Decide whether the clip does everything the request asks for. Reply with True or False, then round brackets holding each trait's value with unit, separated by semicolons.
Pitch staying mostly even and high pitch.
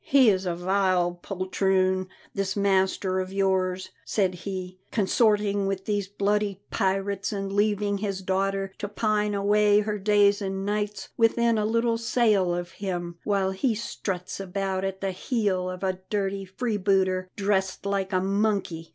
True (1.6 semitones; 195 Hz)